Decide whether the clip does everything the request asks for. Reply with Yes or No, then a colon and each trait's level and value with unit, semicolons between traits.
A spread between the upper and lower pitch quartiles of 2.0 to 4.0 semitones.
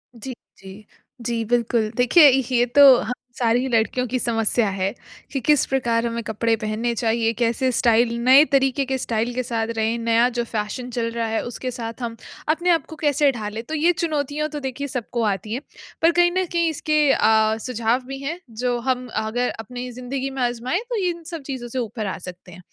Yes: average, 2.9 semitones